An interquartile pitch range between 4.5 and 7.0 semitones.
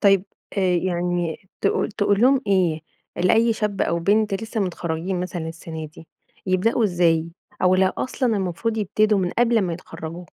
No: average, 3.6 semitones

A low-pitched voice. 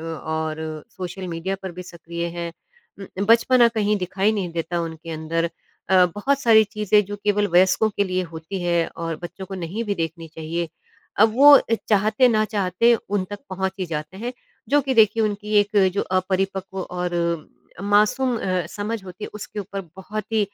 No: high, 190 Hz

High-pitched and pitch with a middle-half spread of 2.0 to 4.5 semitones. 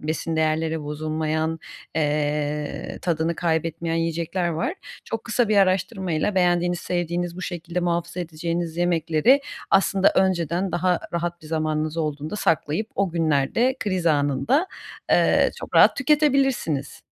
No: medium, 170 Hz; average, 2.8 semitones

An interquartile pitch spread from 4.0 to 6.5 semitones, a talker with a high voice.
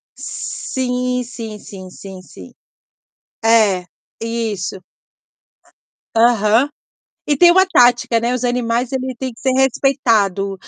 No: average, 3.3 semitones; high, 235 Hz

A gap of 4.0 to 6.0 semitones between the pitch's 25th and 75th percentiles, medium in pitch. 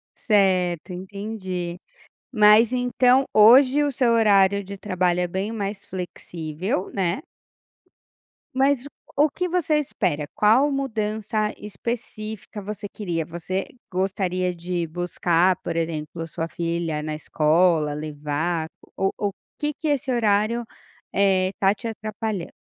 No: average, 4.3 semitones; high, 195 Hz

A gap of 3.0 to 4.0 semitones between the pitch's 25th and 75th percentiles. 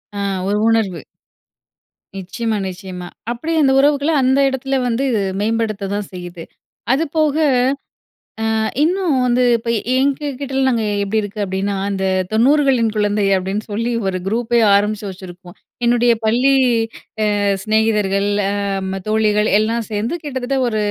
No: average, 4.6 semitones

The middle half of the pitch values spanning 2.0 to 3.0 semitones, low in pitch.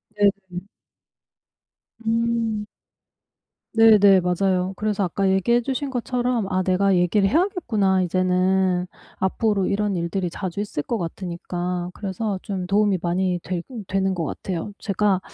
No: narrow, 2.6 semitones; high, 190 Hz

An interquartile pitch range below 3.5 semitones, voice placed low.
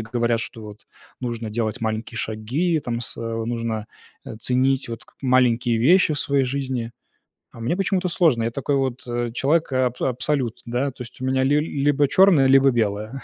Yes: average, 3.1 semitones; low, 125 Hz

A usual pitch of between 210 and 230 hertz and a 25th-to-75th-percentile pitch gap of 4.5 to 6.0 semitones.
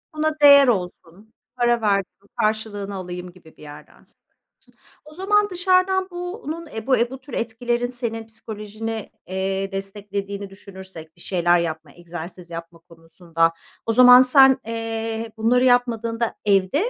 Yes: high, 220 Hz; average, 4.9 semitones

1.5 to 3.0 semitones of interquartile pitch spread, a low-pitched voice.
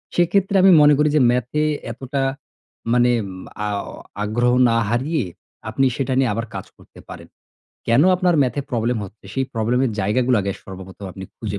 No: average, 3.9 semitones; low, 125 Hz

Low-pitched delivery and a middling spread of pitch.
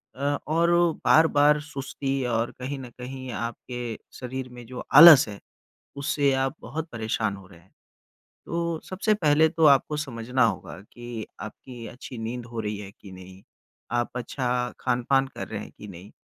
Yes: low, 125 Hz; average, 4.0 semitones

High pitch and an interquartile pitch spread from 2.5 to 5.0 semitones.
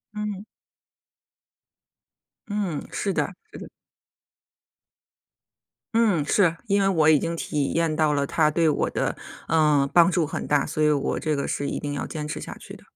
No: medium, 155 Hz; average, 3.5 semitones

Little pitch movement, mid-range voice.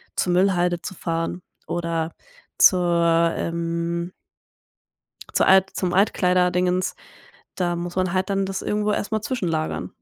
Yes: narrow, 1.9 semitones; medium, 180 Hz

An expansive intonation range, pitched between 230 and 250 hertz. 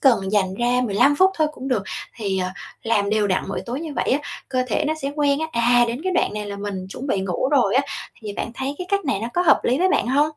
Yes: wide, 5.8 semitones; high, 245 Hz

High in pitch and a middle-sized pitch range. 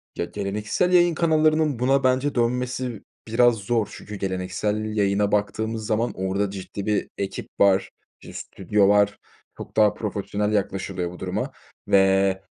No: low, 105 Hz; average, 3.7 semitones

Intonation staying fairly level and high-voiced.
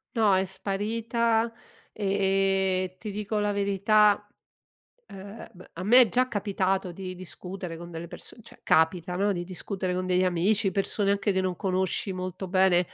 Yes: narrow, 1.9 semitones; high, 195 Hz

